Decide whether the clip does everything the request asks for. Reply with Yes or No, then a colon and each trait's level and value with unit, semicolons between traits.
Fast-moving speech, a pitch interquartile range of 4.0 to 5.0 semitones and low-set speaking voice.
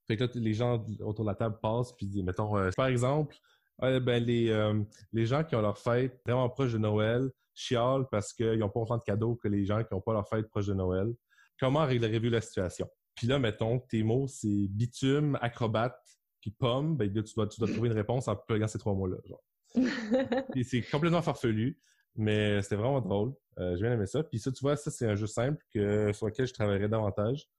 No: fast, 235 wpm; average, 3.2 semitones; low, 115 Hz